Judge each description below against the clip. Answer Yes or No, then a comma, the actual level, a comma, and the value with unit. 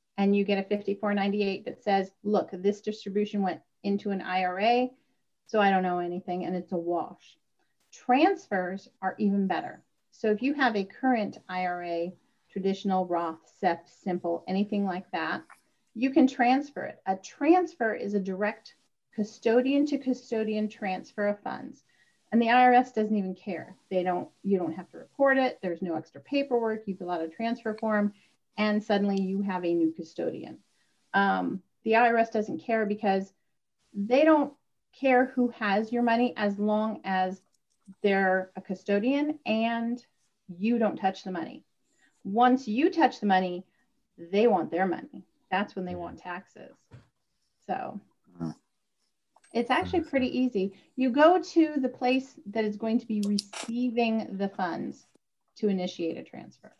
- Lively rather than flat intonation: No, average, 4.3 semitones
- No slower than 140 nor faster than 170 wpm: Yes, average, 155 wpm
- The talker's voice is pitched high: Yes, high, 205 Hz